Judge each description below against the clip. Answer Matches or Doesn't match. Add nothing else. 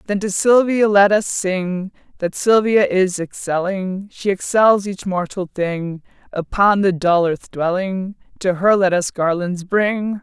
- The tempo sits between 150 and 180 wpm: Matches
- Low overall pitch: Doesn't match